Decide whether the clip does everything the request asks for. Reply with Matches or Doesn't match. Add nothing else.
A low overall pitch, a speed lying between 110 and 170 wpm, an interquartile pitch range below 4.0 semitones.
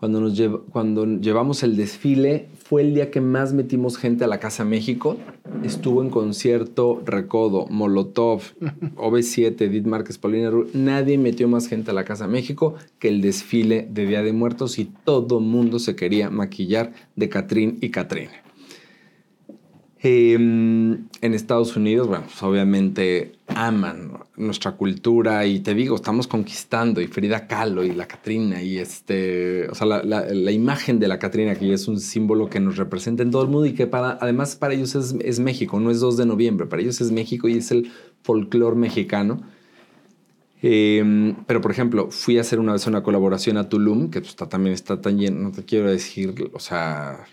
Doesn't match